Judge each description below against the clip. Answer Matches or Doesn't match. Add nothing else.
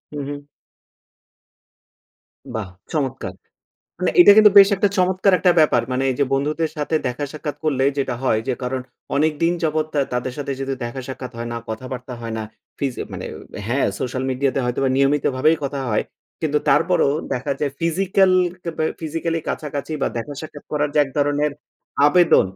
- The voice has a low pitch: Doesn't match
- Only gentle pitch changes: Doesn't match